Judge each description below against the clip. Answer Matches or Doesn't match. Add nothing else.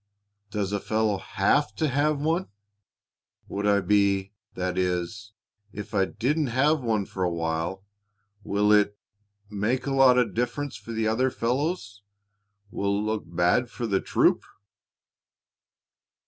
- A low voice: Matches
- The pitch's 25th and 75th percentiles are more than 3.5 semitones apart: Matches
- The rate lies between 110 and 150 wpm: Matches